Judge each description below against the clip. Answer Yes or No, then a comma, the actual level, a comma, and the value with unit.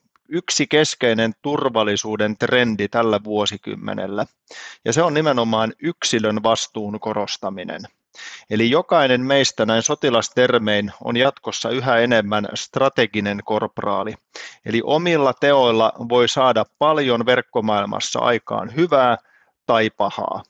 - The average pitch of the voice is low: Yes, low, 115 Hz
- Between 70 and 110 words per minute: Yes, average, 100 wpm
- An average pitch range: Yes, average, 4.2 semitones